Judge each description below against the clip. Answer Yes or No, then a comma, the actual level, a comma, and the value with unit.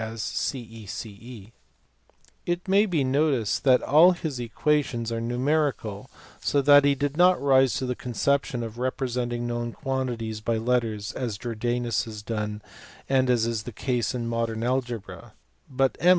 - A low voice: Yes, low, 120 Hz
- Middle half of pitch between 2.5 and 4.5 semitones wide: Yes, average, 2.9 semitones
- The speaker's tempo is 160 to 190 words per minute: No, average, 150 wpm